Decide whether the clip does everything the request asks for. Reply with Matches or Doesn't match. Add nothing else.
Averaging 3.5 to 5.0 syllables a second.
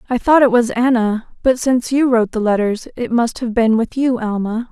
Doesn't match